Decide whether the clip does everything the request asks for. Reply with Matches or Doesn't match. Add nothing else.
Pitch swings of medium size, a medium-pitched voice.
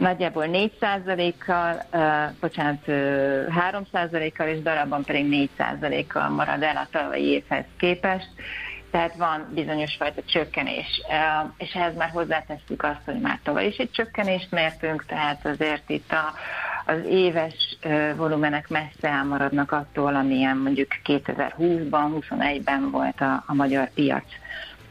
Matches